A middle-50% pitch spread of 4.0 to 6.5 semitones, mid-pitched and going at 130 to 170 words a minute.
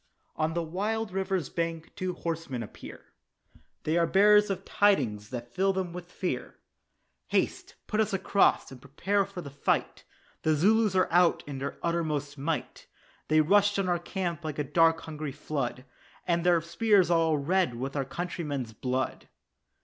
Yes: average, 4.5 semitones; medium, 170 Hz; average, 165 wpm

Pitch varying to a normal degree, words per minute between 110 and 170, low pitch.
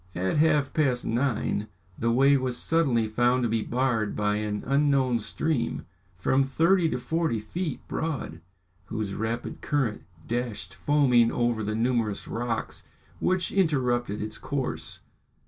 Yes: average, 4.3 semitones; slow, 135 wpm; low, 120 Hz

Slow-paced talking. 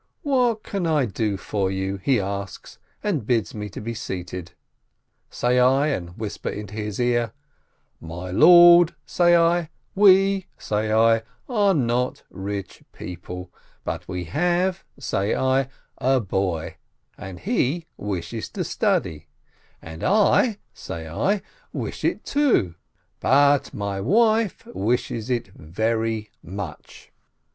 Yes: slow, 125 wpm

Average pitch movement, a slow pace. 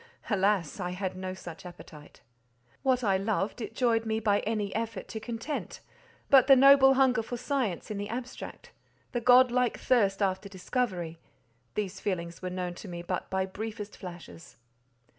No: average, 4.6 semitones; average, 155 wpm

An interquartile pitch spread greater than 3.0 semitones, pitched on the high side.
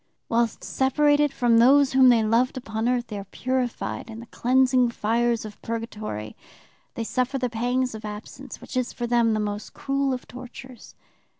No: narrow, 2.5 semitones; high, 240 Hz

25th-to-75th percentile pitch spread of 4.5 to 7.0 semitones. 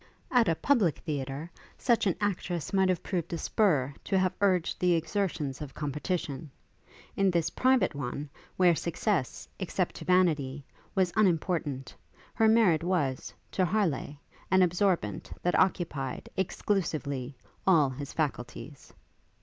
Yes: average, 4.8 semitones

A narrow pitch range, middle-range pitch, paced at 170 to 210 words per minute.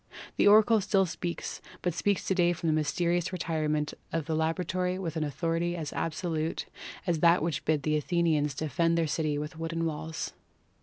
Yes: narrow, 2.1 semitones; medium, 165 Hz; average, 175 wpm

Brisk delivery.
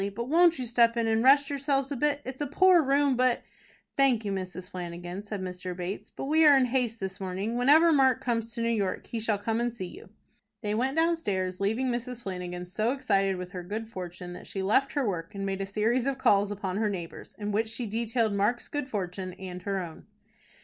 Yes: fast, 225 wpm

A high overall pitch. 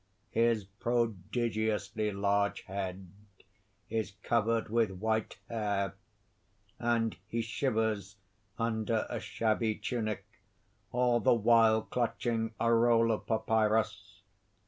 No: low, 110 Hz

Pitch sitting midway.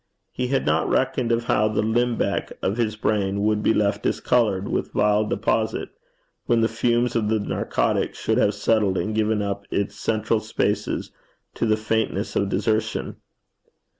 No: low, 110 Hz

